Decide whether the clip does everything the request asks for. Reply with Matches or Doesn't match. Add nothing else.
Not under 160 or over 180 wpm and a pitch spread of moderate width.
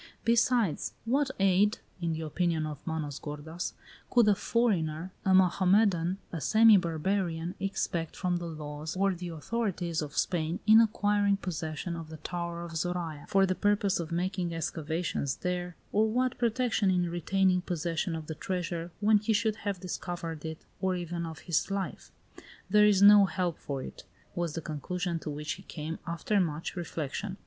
Matches